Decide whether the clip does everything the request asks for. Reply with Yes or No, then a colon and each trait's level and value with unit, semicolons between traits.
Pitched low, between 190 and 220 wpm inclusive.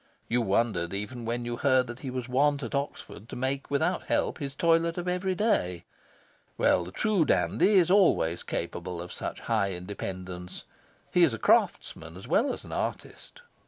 No: low, 120 Hz; average, 170 wpm